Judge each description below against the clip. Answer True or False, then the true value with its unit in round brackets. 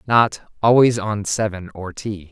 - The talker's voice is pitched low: True (105 Hz)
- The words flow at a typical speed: True (155 wpm)